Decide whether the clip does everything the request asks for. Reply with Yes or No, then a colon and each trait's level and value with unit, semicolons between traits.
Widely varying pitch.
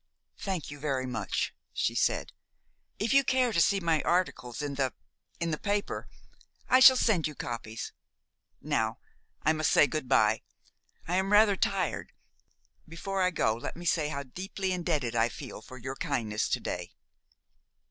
Yes: wide, 6.7 semitones